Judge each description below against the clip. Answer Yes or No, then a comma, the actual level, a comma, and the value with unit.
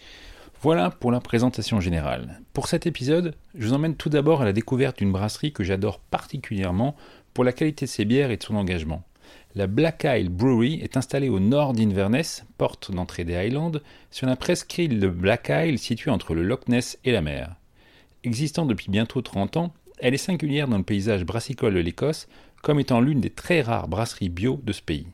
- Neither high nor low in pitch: No, low, 120 Hz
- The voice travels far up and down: Yes, wide, 6.0 semitones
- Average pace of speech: Yes, average, 200 wpm